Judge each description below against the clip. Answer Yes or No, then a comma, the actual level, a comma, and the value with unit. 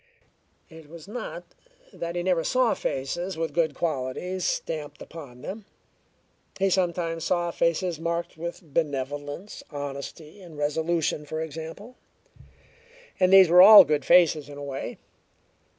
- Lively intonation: No, average, 3.4 semitones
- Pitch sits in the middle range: Yes, medium, 165 Hz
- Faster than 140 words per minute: No, slow, 135 wpm